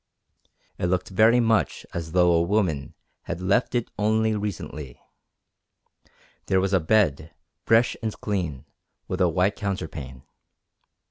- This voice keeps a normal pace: No, slow, 130 wpm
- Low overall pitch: Yes, very low, 95 Hz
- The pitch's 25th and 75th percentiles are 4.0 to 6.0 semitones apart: Yes, average, 4.5 semitones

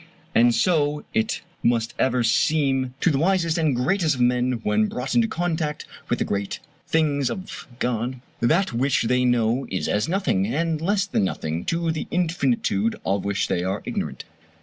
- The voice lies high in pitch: No, low, 135 Hz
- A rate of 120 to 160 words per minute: No, average, 170 wpm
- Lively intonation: Yes, wide, 6.0 semitones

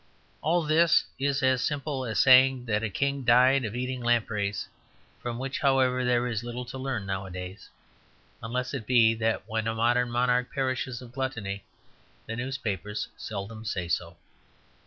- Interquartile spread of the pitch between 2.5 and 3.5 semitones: Yes, average, 2.9 semitones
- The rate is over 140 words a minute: Yes, average, 155 wpm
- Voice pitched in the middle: No, low, 120 Hz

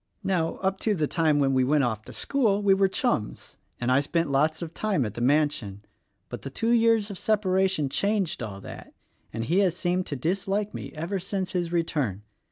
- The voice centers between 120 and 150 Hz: No, medium, 170 Hz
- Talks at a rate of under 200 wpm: No, fast, 205 wpm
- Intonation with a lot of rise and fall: Yes, wide, 6.2 semitones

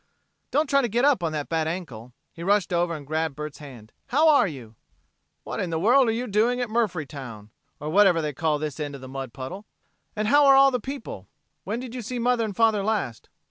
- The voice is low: No, medium, 185 Hz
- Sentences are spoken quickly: Yes, fast, 230 wpm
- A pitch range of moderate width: No, wide, 8.1 semitones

